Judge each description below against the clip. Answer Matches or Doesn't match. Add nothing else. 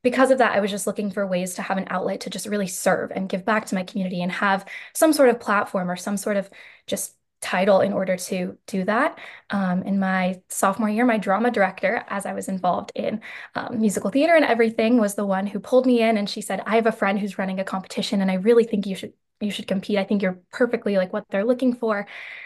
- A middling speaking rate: Doesn't match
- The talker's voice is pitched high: Matches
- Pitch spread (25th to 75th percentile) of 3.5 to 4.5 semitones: Doesn't match